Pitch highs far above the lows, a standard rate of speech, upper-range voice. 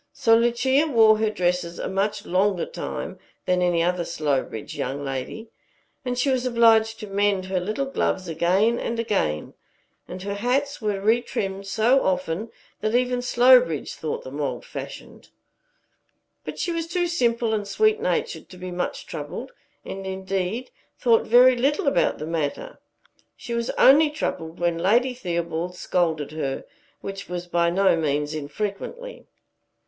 Yes: wide, 5.7 semitones; average, 150 wpm; high, 200 Hz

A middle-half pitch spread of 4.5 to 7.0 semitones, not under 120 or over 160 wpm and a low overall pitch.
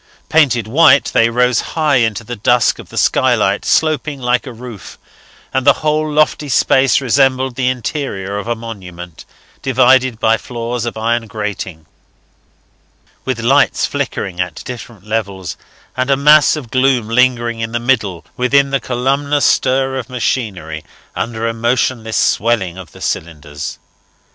No: average, 3.2 semitones; average, 150 wpm; low, 120 Hz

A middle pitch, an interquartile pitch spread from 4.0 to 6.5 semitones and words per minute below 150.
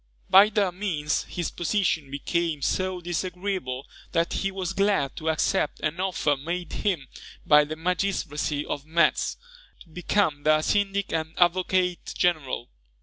No: medium, 175 Hz; average, 3.6 semitones; average, 140 wpm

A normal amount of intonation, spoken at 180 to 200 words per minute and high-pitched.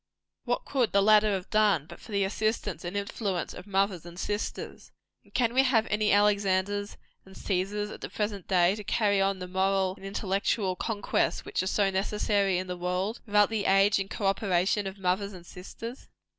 No: narrow, 1.8 semitones; average, 195 wpm; high, 200 Hz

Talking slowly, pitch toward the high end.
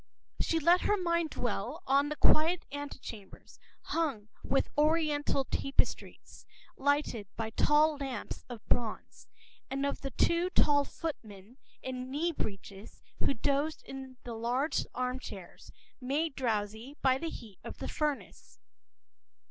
Yes: slow, 130 wpm; very high, 275 Hz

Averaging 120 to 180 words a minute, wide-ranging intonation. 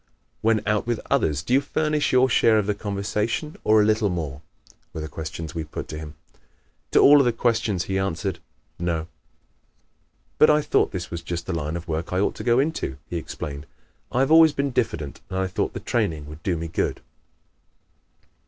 No: average, 200 wpm; wide, 6.6 semitones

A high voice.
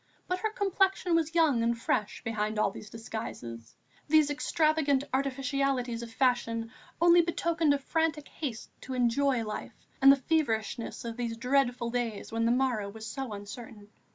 Yes: very high, 250 Hz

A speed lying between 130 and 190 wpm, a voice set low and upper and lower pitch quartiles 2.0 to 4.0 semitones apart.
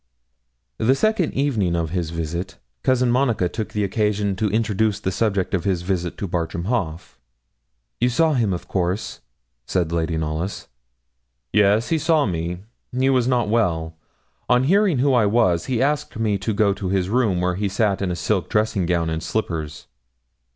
No: average, 170 wpm; low, 100 Hz; average, 5.2 semitones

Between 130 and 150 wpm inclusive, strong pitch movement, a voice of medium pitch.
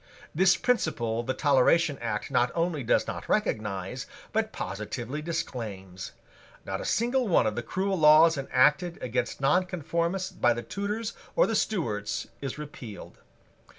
Yes: average, 140 wpm; wide, 7.1 semitones; medium, 145 Hz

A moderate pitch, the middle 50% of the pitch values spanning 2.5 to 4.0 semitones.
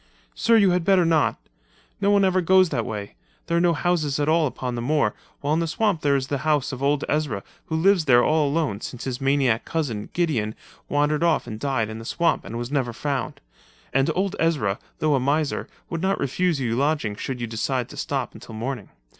No: medium, 145 Hz; average, 5.2 semitones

